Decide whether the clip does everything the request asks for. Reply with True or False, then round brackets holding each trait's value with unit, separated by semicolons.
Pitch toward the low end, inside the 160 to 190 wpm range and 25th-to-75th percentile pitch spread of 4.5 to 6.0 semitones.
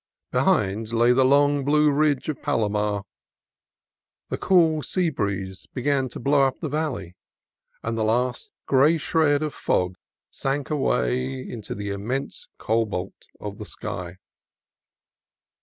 False (130 Hz; 135 wpm; 5.5 semitones)